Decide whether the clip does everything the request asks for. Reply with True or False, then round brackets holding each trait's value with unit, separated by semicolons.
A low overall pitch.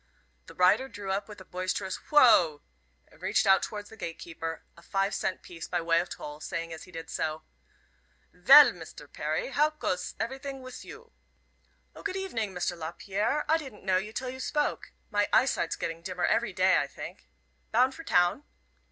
False (195 Hz)